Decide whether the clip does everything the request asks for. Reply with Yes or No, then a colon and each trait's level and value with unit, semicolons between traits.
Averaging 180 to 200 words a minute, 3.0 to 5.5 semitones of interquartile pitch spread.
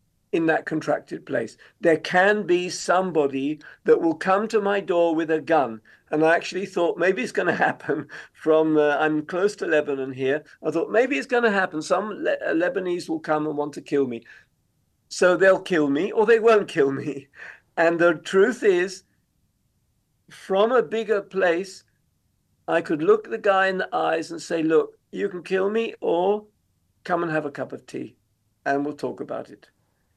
Yes: average, 190 wpm; average, 4.7 semitones